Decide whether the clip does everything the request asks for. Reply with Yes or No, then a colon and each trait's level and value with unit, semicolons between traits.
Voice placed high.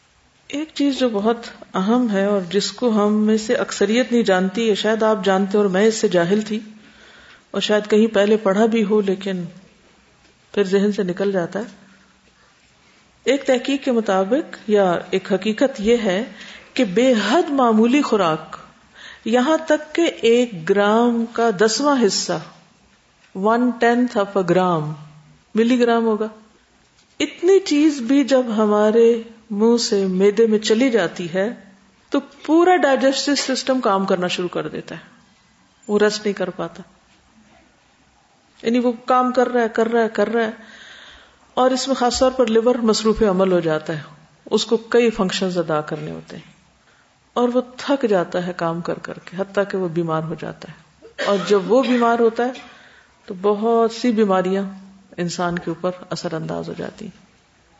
Yes: high, 215 Hz